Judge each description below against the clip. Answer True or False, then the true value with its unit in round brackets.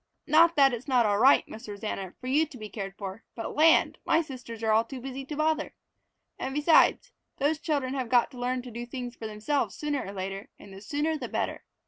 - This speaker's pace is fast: True (220 wpm)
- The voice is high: True (255 Hz)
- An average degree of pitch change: True (5.0 semitones)